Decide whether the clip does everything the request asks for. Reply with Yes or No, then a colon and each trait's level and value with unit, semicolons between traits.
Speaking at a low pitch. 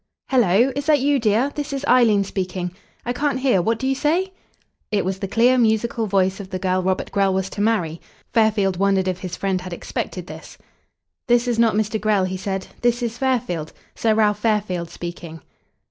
No: high, 210 Hz